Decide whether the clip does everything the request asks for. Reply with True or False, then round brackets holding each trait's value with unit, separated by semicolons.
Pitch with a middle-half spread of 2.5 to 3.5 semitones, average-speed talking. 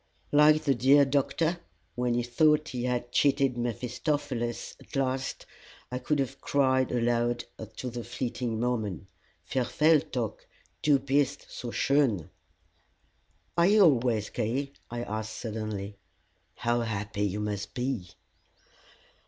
False (3.2 semitones; 125 wpm)